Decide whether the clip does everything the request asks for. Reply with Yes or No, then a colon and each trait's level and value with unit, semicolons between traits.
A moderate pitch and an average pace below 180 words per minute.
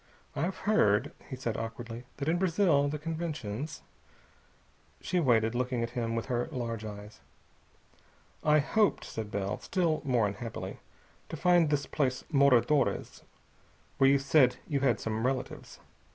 No: low, 130 Hz; average, 140 wpm